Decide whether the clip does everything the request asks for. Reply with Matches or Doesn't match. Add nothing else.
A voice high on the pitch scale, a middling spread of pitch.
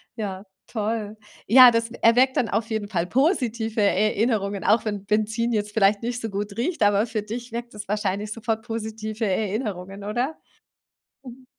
Doesn't match